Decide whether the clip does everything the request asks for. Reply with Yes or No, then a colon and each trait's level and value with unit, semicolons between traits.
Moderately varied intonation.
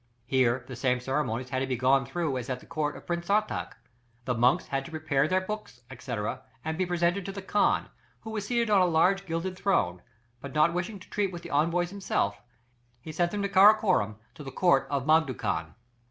No: wide, 6.1 semitones